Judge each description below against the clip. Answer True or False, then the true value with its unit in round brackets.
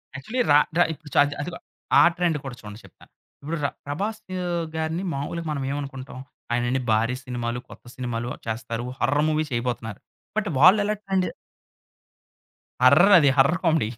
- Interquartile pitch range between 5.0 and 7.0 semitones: True (5.4 semitones)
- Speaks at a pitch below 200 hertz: True (140 Hz)